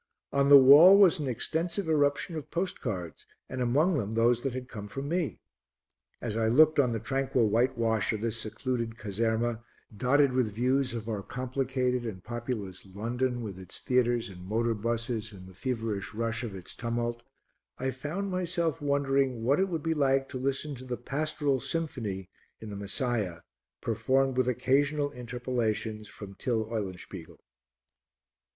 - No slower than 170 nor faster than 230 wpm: No, average, 160 wpm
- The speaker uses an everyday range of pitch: Yes, average, 3.8 semitones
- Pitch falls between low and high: No, low, 125 Hz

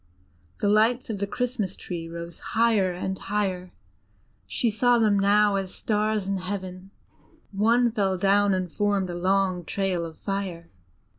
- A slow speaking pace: No, average, 150 wpm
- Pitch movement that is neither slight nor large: No, narrow, 2.3 semitones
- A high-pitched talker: Yes, high, 195 Hz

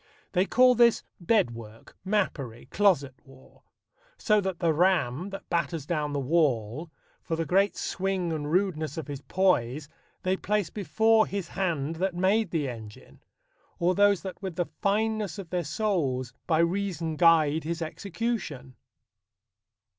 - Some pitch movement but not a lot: Yes, average, 5.0 semitones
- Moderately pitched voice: Yes, medium, 170 Hz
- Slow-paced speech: No, average, 145 wpm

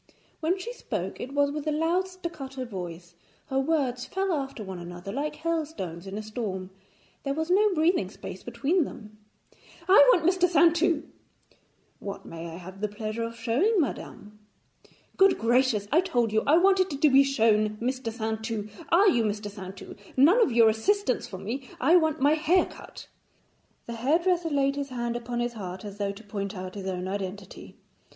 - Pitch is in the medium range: No, high, 245 Hz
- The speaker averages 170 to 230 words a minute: Yes, average, 180 wpm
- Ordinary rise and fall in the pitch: No, wide, 7.4 semitones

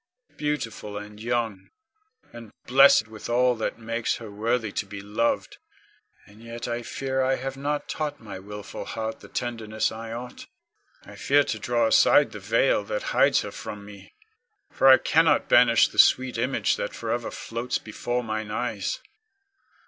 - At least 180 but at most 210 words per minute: No, average, 165 wpm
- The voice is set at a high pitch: No, low, 115 Hz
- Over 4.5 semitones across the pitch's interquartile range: No, average, 2.7 semitones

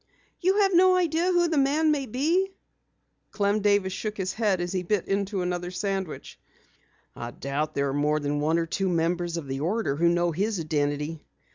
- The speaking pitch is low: No, medium, 185 Hz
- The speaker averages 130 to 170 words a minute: No, average, 190 wpm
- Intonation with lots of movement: Yes, wide, 6.5 semitones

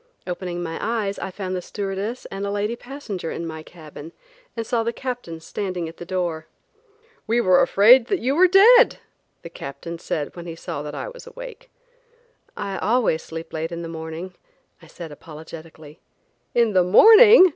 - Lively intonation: Yes, wide, 6.3 semitones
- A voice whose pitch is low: No, medium, 185 Hz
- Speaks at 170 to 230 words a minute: Yes, average, 180 wpm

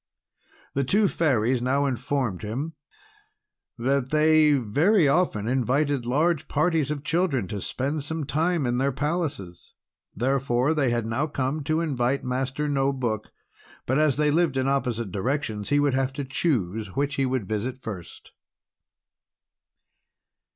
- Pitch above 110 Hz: Yes, low, 135 Hz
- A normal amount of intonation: Yes, average, 3.6 semitones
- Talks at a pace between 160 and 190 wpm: No, average, 145 wpm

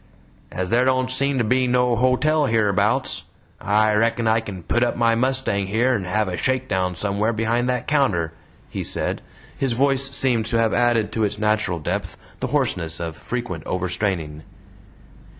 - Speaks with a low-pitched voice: Yes, low, 115 Hz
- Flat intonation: No, average, 4.2 semitones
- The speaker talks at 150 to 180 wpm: Yes, average, 170 wpm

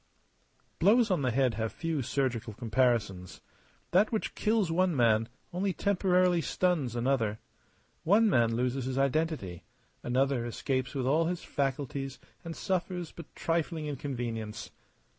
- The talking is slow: Yes, slow, 130 wpm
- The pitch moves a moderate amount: No, wide, 6.2 semitones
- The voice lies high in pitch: No, low, 135 Hz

